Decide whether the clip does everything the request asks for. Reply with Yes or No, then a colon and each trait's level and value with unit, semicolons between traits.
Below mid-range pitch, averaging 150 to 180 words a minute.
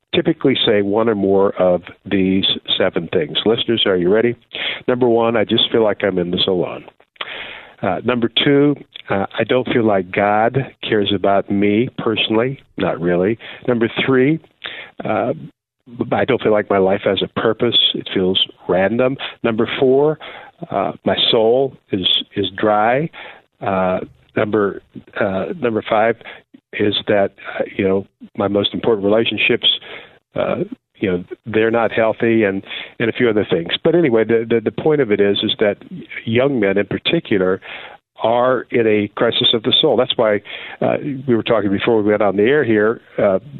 Yes: low, 110 Hz; average, 170 wpm